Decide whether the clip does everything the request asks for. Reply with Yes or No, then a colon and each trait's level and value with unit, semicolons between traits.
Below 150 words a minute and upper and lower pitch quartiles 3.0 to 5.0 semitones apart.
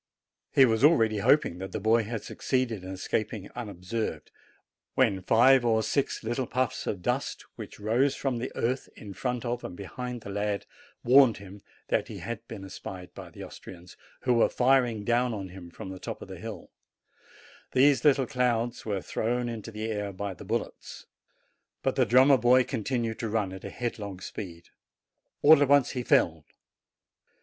No: average, 175 wpm; average, 3.9 semitones